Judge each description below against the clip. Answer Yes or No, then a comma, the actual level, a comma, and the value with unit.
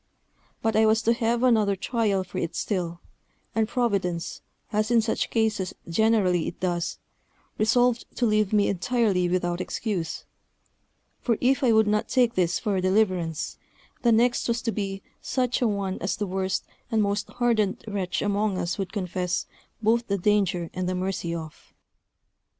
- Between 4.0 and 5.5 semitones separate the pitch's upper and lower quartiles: No, average, 3.6 semitones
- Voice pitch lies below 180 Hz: No, high, 205 Hz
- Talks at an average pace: Yes, average, 165 wpm